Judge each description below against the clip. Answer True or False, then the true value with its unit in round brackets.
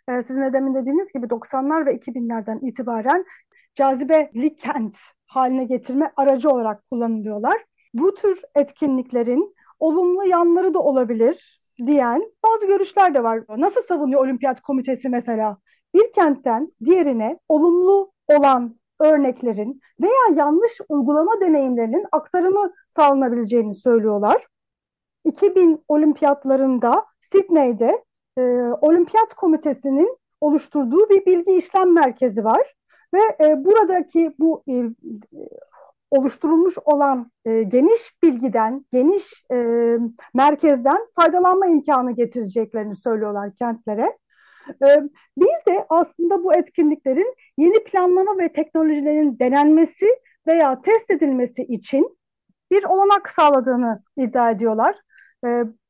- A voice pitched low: False (295 Hz)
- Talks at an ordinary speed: True (105 wpm)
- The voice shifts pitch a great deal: True (6.2 semitones)